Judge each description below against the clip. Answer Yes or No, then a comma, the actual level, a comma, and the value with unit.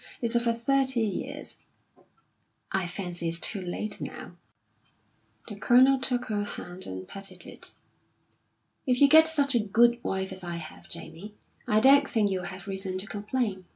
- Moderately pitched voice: No, high, 210 Hz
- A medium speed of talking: Yes, average, 160 wpm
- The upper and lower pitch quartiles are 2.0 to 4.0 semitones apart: No, average, 4.6 semitones